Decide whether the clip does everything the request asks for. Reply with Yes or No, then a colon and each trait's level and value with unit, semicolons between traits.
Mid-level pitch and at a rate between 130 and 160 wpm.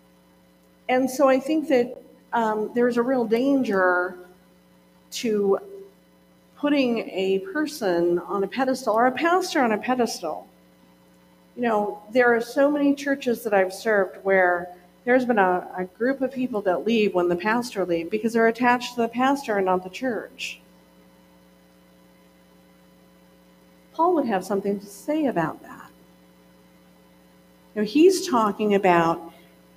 No: high, 195 Hz; average, 140 wpm